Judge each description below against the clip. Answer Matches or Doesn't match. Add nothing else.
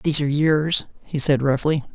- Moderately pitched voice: Matches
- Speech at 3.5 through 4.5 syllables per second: Doesn't match